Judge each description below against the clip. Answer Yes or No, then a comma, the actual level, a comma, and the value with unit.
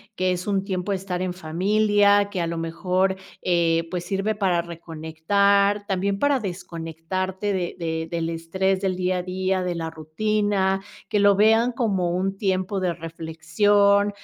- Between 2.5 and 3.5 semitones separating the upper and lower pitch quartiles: Yes, average, 2.9 semitones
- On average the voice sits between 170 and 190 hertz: Yes, medium, 185 Hz